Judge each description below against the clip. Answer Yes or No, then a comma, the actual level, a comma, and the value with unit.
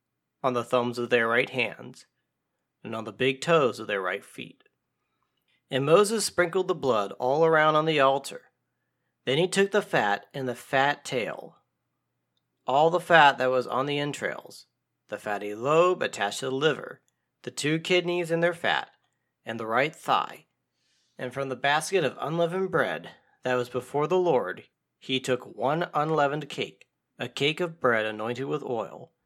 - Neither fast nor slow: Yes, average, 170 wpm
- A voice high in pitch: No, low, 135 Hz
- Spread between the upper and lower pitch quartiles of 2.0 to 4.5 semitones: No, average, 5.3 semitones